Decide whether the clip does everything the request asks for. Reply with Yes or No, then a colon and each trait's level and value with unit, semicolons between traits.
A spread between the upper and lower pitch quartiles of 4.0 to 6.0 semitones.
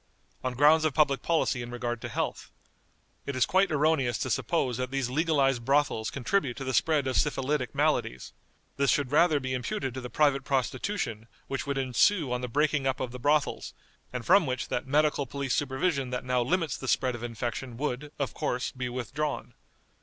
No: average, 3.0 semitones